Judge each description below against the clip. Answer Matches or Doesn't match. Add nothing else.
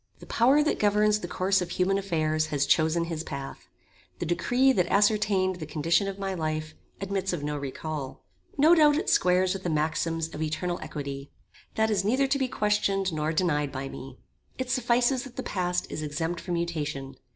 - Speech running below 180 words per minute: Doesn't match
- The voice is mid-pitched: Matches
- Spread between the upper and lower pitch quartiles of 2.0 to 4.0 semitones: Doesn't match